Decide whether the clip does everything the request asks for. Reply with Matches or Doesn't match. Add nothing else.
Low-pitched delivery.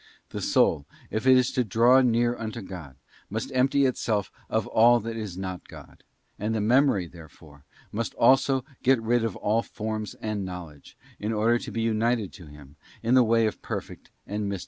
Matches